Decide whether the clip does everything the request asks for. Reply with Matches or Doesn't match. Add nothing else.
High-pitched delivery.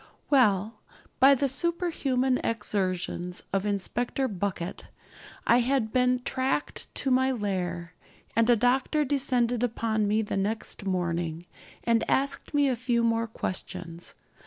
Matches